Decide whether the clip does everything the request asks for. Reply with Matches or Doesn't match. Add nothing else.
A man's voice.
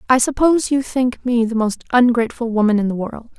Doesn't match